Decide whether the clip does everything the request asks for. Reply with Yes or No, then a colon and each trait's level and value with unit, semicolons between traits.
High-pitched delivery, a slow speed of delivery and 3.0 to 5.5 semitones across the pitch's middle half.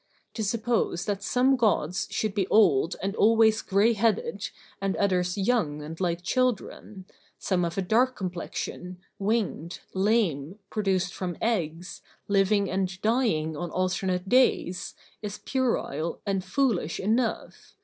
Yes: high, 195 Hz; slow, 130 wpm; average, 3.8 semitones